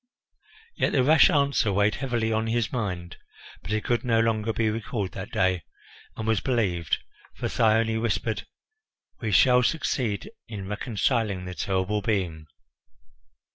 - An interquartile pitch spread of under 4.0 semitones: Yes, average, 3.0 semitones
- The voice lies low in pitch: Yes, low, 110 Hz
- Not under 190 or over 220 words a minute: No, average, 140 wpm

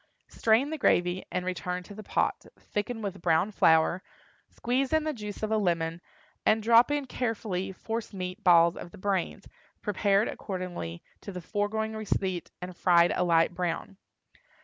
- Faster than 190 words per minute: No, average, 165 wpm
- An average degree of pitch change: Yes, average, 3.7 semitones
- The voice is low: No, high, 195 Hz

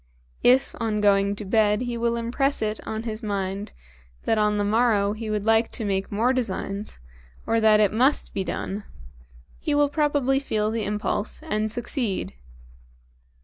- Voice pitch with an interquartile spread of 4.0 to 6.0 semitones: No, narrow, 2.6 semitones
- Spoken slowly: No, average, 165 wpm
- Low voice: No, high, 220 Hz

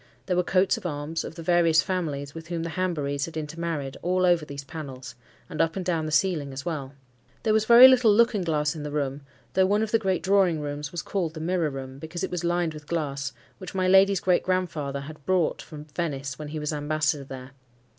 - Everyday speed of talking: No, fast, 225 wpm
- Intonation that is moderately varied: Yes, average, 3.9 semitones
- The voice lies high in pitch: No, medium, 160 Hz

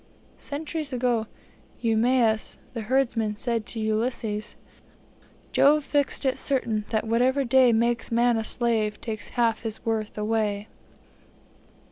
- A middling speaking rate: No, slow, 120 wpm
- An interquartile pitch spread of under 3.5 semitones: Yes, average, 2.7 semitones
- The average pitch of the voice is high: Yes, high, 230 Hz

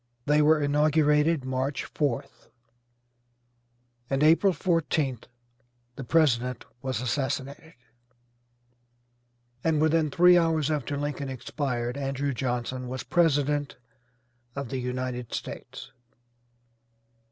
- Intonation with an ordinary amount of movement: Yes, average, 3.1 semitones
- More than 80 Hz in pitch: Yes, medium, 140 Hz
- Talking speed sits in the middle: No, slow, 95 wpm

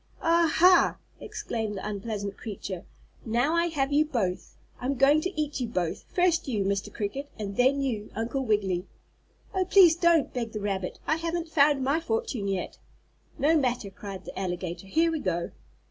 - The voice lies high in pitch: Yes, very high, 250 Hz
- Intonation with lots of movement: Yes, wide, 7.9 semitones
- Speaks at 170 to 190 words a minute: Yes, average, 175 wpm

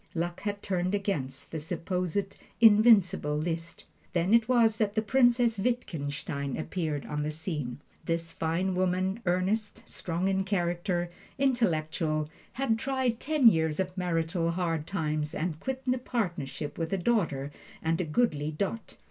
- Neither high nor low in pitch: Yes, medium, 180 Hz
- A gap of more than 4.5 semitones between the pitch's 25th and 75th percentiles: Yes, average, 5.1 semitones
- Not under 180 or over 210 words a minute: No, average, 145 wpm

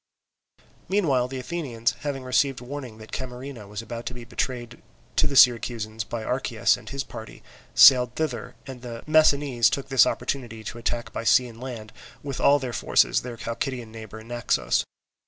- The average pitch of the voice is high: No, low, 125 Hz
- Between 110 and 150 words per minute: No, average, 170 wpm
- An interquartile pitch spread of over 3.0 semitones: No, average, 2.7 semitones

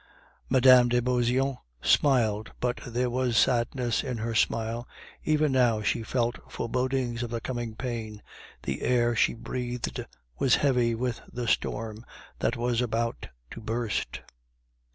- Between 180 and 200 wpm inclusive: No, slow, 135 wpm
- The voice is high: No, low, 120 Hz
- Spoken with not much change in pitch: Yes, narrow, 1.6 semitones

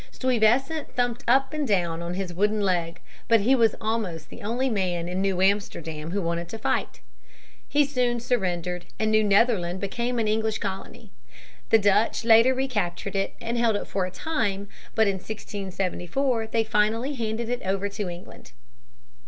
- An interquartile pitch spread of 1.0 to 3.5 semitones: No, average, 4.1 semitones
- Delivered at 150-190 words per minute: Yes, average, 170 wpm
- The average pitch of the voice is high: Yes, high, 210 Hz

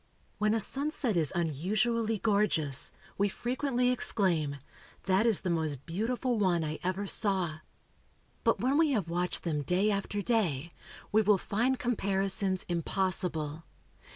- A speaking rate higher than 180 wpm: No, slow, 135 wpm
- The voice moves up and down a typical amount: Yes, average, 4.8 semitones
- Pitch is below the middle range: No, high, 195 Hz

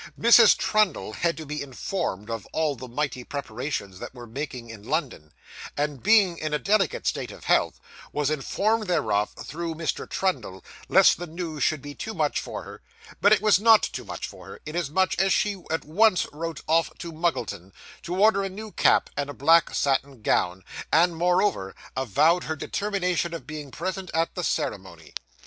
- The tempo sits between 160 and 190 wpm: Yes, average, 180 wpm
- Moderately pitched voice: Yes, medium, 160 Hz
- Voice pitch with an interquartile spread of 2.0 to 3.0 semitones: No, wide, 5.5 semitones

